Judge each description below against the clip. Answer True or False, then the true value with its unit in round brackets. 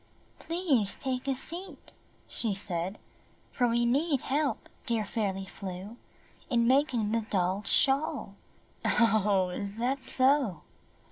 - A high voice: True (235 Hz)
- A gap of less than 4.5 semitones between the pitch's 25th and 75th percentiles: False (5.1 semitones)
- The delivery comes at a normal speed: False (120 wpm)